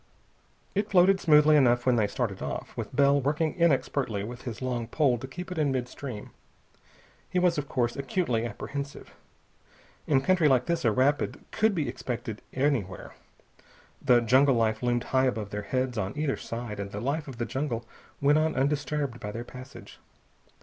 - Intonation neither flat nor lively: Yes, average, 3.8 semitones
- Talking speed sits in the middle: Yes, average, 175 wpm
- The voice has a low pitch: Yes, low, 130 Hz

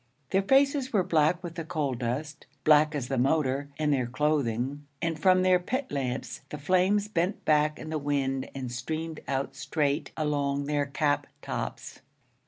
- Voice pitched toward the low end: No, medium, 150 Hz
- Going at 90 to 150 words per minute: No, average, 170 wpm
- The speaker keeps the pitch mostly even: No, average, 3.3 semitones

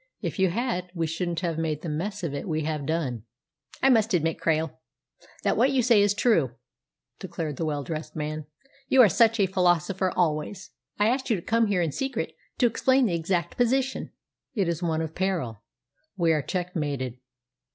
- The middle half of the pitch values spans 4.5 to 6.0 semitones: Yes, average, 4.9 semitones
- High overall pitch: No, medium, 175 Hz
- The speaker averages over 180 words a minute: Yes, average, 195 wpm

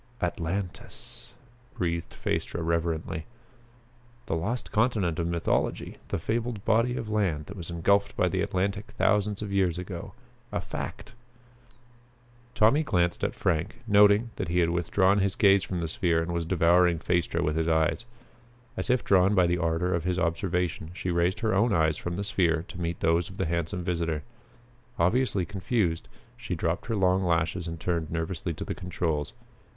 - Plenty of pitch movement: No, average, 3.2 semitones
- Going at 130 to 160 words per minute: No, average, 170 wpm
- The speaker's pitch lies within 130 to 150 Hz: No, very low, 90 Hz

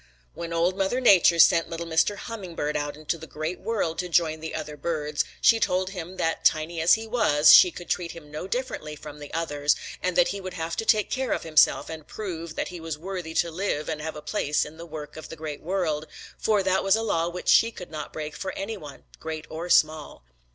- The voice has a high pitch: No, medium, 165 Hz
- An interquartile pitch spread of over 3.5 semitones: No, average, 3.2 semitones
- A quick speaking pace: Yes, fast, 235 wpm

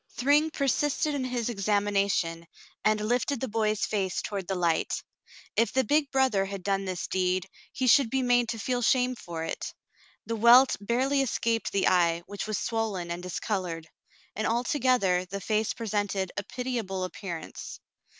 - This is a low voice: No, high, 215 Hz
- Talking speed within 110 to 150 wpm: No, average, 160 wpm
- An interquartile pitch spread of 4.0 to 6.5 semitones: Yes, average, 4.7 semitones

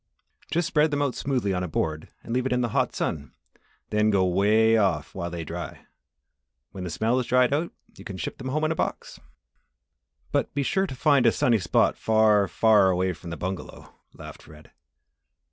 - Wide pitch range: Yes, wide, 5.9 semitones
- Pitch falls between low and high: No, low, 110 Hz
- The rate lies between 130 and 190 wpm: No, average, 200 wpm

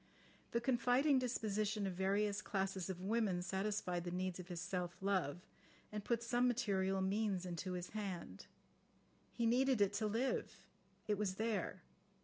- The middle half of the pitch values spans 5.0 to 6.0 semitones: No, average, 3.2 semitones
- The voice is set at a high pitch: Yes, high, 200 Hz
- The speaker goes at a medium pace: Yes, average, 150 wpm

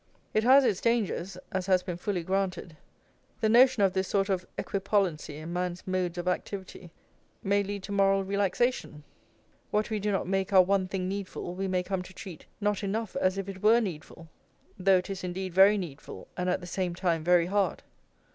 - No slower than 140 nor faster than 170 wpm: No, average, 195 wpm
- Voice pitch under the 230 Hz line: Yes, high, 190 Hz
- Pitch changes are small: Yes, narrow, 1.8 semitones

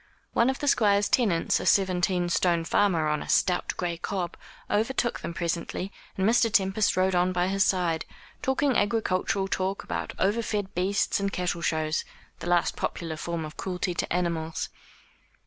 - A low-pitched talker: No, medium, 185 Hz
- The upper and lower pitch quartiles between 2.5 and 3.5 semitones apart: Yes, average, 2.8 semitones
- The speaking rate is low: No, average, 165 wpm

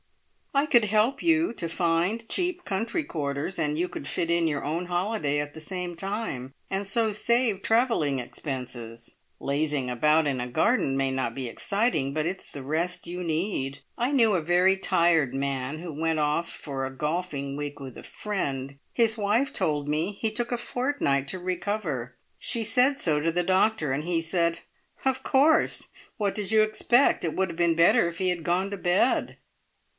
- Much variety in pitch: Yes, wide, 6.5 semitones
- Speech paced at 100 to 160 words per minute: No, average, 185 wpm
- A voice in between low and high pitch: Yes, medium, 170 Hz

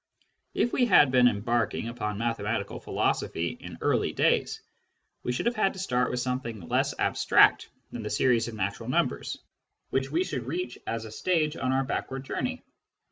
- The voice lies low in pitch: Yes, low, 125 Hz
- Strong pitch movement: No, average, 2.8 semitones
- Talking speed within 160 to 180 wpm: Yes, average, 175 wpm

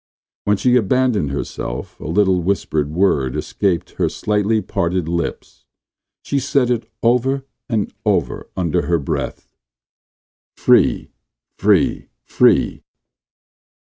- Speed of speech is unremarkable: No, slow, 105 wpm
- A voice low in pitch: Yes, low, 100 Hz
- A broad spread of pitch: Yes, wide, 5.9 semitones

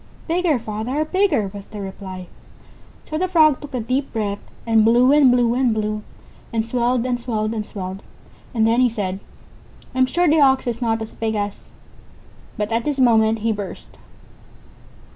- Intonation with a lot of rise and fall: No, average, 3.4 semitones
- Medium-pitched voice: No, high, 230 Hz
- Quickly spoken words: No, average, 180 wpm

